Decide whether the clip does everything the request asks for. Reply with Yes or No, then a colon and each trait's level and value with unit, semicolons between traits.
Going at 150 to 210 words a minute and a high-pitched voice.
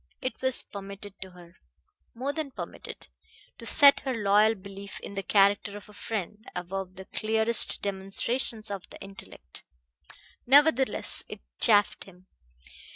No: average, 140 wpm; high, 205 Hz